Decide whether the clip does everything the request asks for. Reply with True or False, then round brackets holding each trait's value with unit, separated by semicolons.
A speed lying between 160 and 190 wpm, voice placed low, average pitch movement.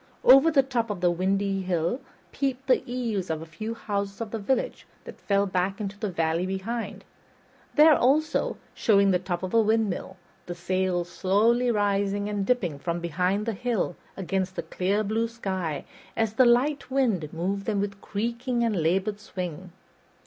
False (170 wpm; 200 Hz; 3.9 semitones)